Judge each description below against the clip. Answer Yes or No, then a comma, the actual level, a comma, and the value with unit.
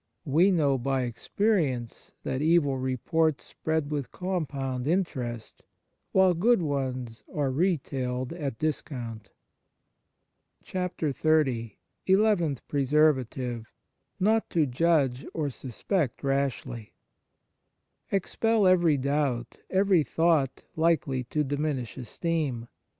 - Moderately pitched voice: Yes, medium, 145 Hz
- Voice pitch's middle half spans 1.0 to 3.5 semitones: No, average, 4.7 semitones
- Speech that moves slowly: Yes, slow, 100 wpm